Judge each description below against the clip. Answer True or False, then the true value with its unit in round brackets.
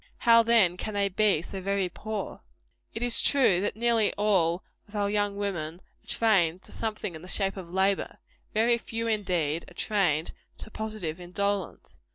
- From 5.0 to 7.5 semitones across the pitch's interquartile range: False (3.5 semitones)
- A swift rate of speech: False (175 wpm)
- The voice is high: True (200 Hz)